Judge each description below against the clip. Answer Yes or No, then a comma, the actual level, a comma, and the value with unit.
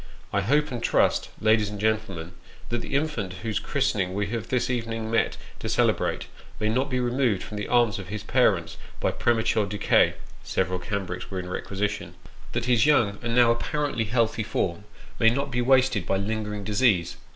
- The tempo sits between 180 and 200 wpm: Yes, average, 185 wpm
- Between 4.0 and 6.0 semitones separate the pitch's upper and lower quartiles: No, average, 3.3 semitones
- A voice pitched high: No, low, 110 Hz